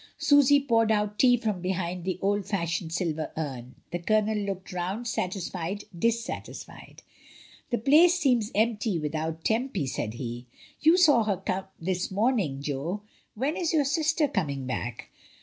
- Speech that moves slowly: No, average, 150 wpm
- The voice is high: Yes, high, 200 Hz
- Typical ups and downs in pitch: No, wide, 6.1 semitones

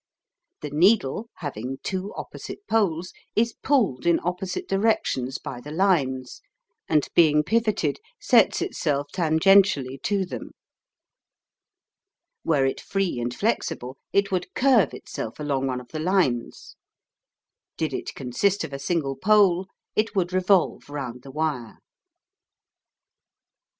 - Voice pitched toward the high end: No, medium, 165 Hz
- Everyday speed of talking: No, slow, 125 wpm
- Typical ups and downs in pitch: No, wide, 6.4 semitones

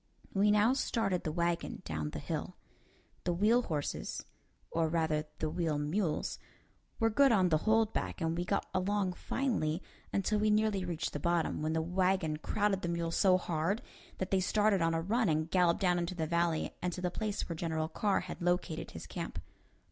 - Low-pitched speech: No, medium, 180 Hz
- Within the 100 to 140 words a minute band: No, average, 195 wpm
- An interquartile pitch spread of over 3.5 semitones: Yes, average, 4.0 semitones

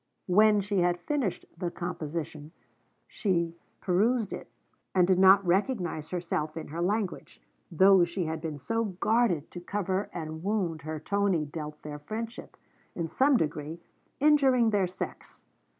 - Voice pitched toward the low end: No, medium, 180 Hz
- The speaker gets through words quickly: No, average, 145 wpm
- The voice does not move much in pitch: No, average, 4.3 semitones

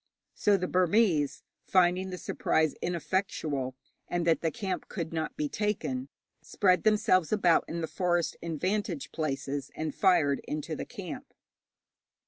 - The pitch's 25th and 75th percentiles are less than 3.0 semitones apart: No, average, 3.8 semitones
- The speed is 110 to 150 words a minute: Yes, average, 140 wpm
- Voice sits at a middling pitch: Yes, medium, 175 Hz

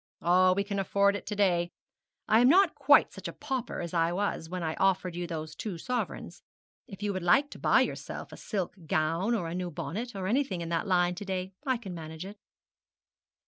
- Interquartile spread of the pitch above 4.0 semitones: No, average, 3.3 semitones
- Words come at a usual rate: No, fast, 220 wpm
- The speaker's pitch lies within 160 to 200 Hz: Yes, medium, 185 Hz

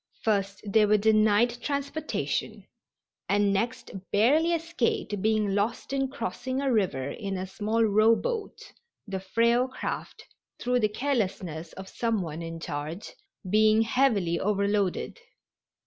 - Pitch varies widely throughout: No, average, 4.1 semitones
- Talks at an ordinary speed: No, slow, 125 wpm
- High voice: Yes, high, 215 Hz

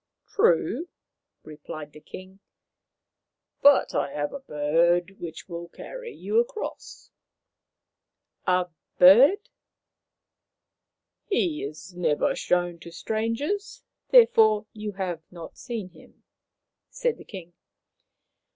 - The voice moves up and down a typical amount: No, wide, 8.9 semitones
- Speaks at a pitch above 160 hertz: Yes, high, 190 Hz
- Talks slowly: Yes, slow, 115 wpm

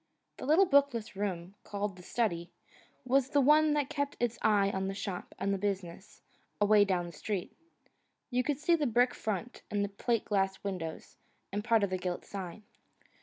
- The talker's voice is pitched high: Yes, high, 205 Hz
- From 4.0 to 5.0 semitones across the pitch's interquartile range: Yes, average, 4.5 semitones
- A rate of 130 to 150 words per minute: No, average, 185 wpm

